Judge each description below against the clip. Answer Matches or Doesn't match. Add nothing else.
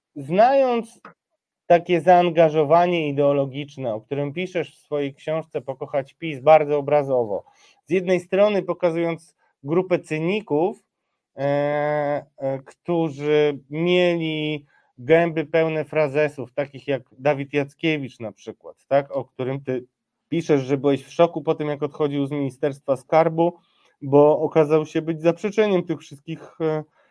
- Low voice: Doesn't match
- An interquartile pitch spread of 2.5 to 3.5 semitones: Matches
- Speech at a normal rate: Matches